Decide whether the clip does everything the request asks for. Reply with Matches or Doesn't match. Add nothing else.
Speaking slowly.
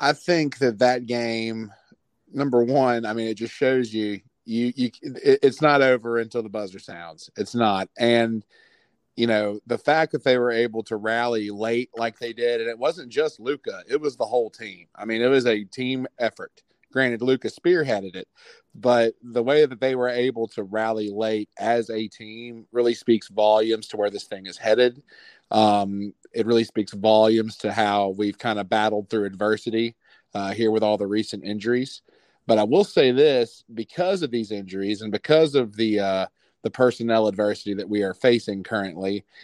Doesn't match